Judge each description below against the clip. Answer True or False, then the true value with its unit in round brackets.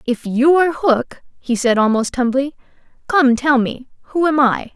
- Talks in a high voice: True (265 Hz)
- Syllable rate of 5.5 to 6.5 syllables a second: False (4.6 syllables/s)